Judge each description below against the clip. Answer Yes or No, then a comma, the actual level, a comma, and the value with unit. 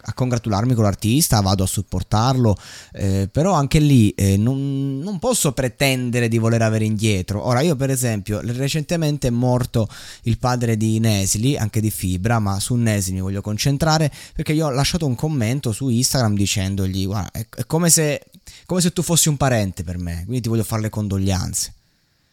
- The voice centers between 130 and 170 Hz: No, low, 115 Hz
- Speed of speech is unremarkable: No, fast, 180 wpm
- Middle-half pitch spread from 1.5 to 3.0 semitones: No, average, 4.8 semitones